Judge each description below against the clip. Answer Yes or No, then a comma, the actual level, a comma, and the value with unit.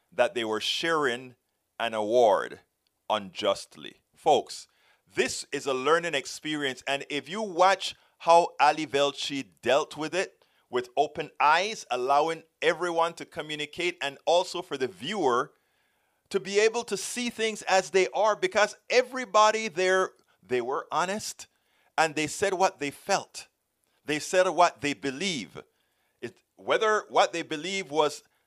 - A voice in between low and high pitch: Yes, medium, 175 Hz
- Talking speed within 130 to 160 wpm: Yes, average, 140 wpm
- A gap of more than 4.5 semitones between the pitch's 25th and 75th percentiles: Yes, wide, 5.6 semitones